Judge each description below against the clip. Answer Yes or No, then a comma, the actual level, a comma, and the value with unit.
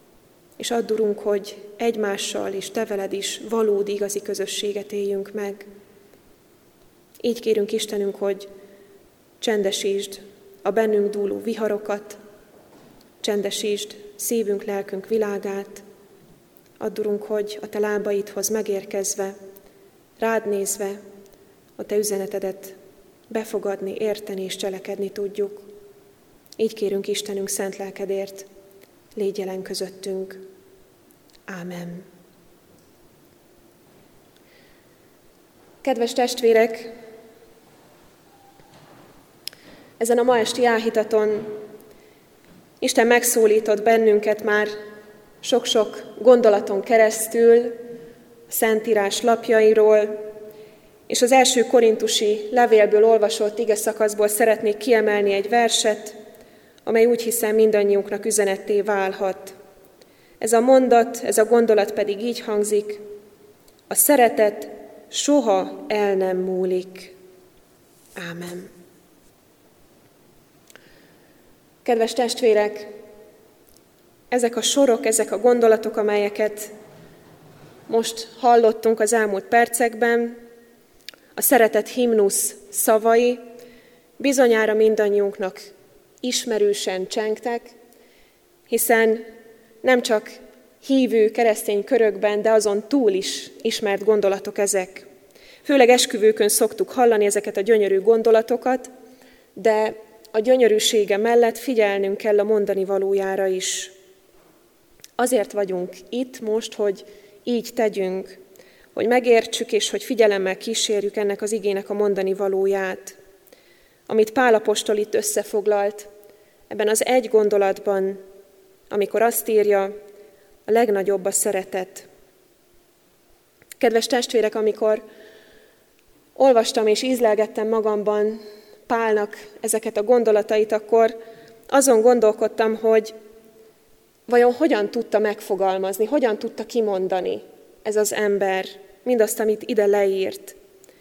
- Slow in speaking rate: Yes, slow, 95 wpm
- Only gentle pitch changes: Yes, narrow, 2.1 semitones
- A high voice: Yes, high, 215 Hz